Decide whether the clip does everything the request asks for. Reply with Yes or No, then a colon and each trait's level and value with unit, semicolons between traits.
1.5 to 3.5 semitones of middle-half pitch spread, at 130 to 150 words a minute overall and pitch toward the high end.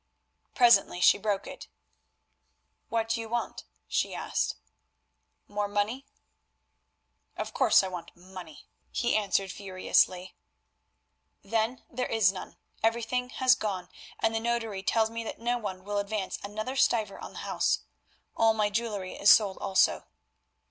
Yes: average, 2.8 semitones; average, 140 wpm; high, 215 Hz